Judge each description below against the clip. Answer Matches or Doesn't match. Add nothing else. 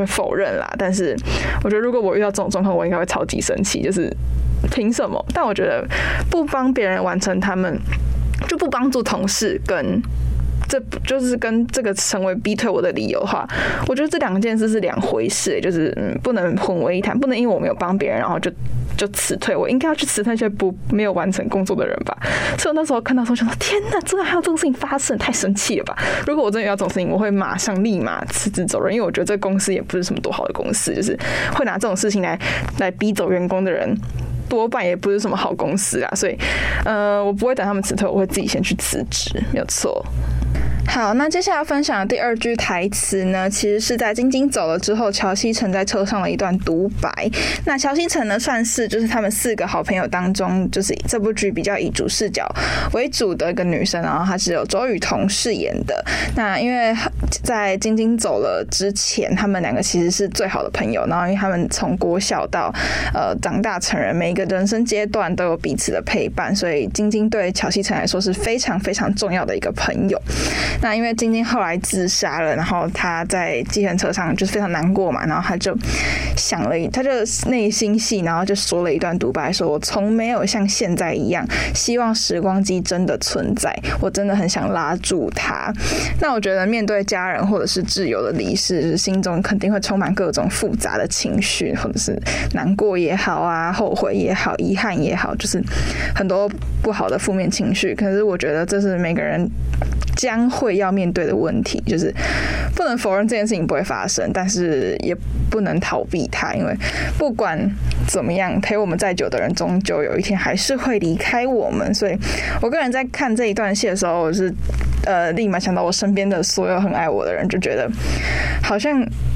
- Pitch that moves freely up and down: Doesn't match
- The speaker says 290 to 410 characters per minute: Matches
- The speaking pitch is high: Matches